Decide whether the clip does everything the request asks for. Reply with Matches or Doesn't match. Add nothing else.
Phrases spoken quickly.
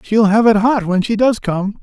Matches